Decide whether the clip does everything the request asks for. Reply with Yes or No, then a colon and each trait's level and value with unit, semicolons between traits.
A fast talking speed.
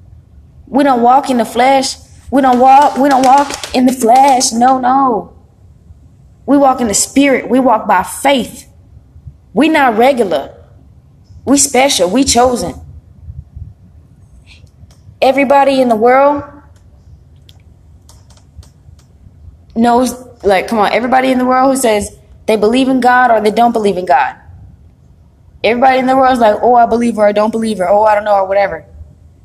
No: average, 155 wpm